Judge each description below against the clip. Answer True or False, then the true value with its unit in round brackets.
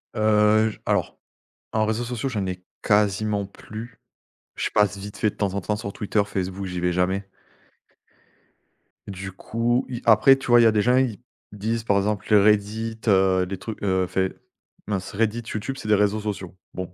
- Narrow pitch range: True (2.3 semitones)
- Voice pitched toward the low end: True (105 Hz)